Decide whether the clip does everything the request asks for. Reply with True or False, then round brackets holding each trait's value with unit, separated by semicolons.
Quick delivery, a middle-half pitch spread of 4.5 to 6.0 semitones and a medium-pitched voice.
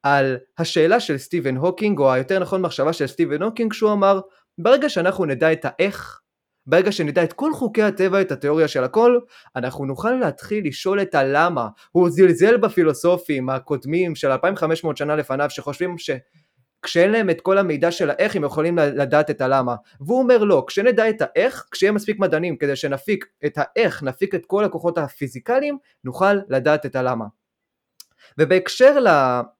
True (160 wpm; 5.4 semitones; 170 Hz)